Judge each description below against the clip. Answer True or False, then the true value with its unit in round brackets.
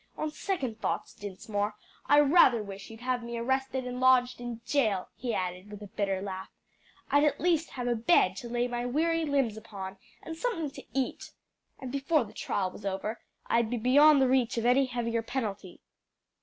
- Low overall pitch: False (245 Hz)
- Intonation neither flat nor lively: True (4.4 semitones)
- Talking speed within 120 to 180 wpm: False (190 wpm)